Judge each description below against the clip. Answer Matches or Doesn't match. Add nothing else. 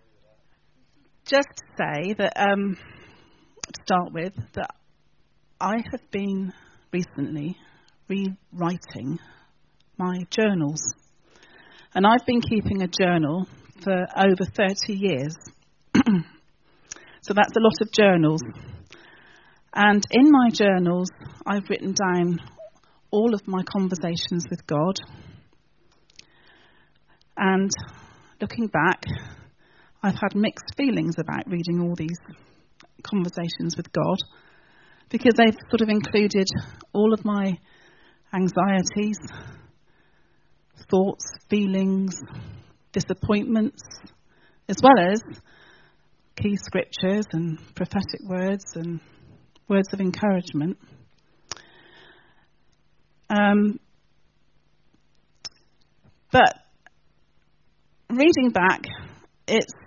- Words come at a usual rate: Doesn't match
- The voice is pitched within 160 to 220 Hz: Matches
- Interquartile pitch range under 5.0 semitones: Matches